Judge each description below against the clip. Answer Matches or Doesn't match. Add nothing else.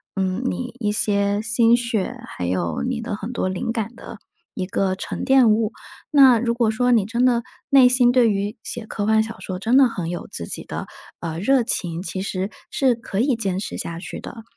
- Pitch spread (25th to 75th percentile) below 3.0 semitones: Doesn't match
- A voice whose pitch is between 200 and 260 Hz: Matches